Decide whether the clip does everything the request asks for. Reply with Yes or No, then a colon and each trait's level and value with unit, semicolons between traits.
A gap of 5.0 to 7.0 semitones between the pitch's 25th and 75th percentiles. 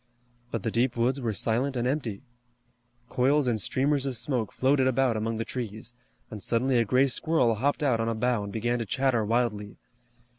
No: average, 2.8 semitones